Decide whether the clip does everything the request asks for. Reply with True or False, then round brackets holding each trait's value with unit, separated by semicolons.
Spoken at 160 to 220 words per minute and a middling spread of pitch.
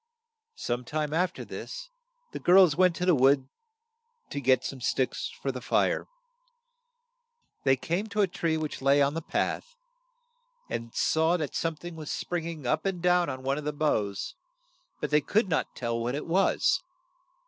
True (180 wpm; 4.7 semitones)